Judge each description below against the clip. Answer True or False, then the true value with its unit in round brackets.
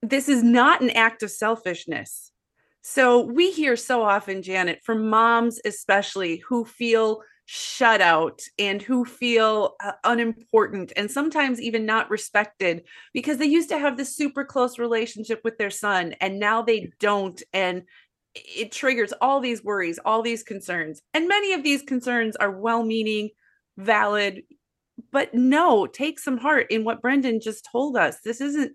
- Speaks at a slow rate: False (160 wpm)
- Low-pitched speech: False (230 Hz)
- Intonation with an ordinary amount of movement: True (4.4 semitones)